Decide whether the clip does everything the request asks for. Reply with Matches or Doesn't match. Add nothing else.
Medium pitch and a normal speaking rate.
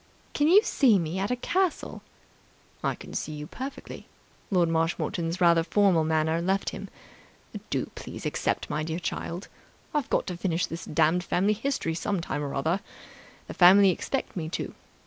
Matches